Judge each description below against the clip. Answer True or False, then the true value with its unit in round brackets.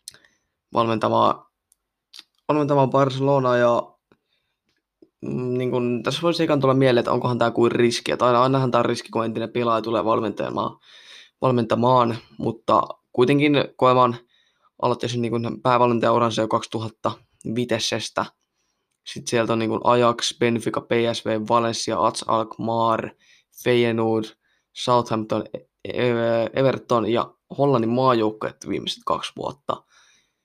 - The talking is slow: False (105 wpm)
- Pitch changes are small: True (1.6 semitones)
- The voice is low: True (120 Hz)